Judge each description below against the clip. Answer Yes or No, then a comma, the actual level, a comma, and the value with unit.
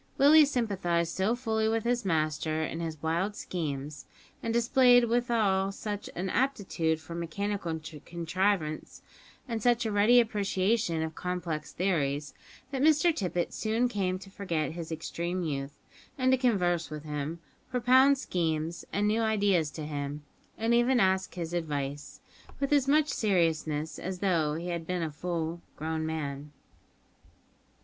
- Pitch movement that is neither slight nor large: No, wide, 5.9 semitones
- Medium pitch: Yes, medium, 180 Hz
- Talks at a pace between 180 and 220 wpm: No, average, 150 wpm